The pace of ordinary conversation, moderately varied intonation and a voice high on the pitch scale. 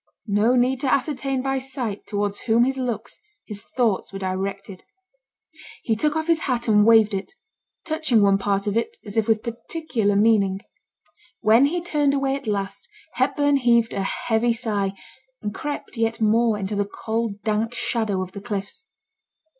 Yes: average, 170 wpm; average, 4.1 semitones; high, 225 Hz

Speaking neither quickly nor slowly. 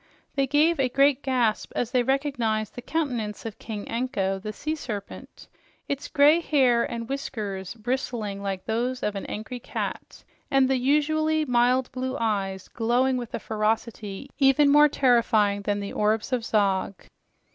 Yes: average, 155 wpm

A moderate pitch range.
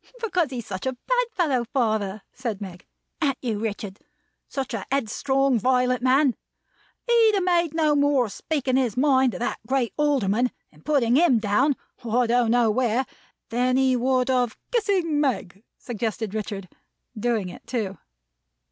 Yes: average, 4.1 semitones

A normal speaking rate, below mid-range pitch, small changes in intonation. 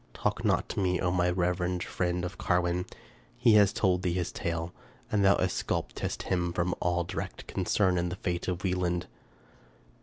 Yes: average, 175 wpm; very low, 90 Hz; narrow, 0.9 semitones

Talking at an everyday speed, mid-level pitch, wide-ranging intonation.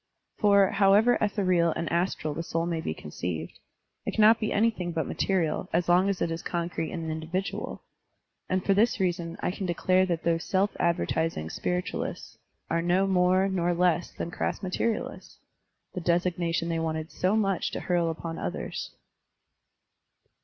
No: average, 160 wpm; medium, 175 Hz; narrow, 2.5 semitones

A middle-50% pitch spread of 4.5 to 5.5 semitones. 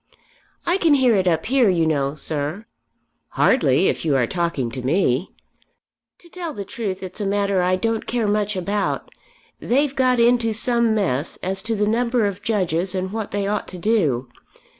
Yes: average, 5.0 semitones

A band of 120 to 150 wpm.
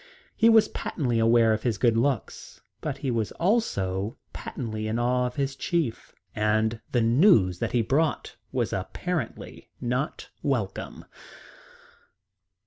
Yes: slow, 135 wpm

